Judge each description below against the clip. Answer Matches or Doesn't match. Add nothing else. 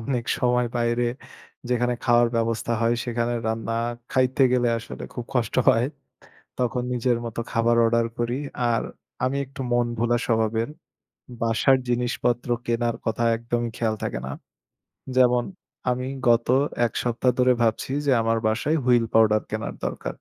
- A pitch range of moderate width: Doesn't match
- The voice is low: Matches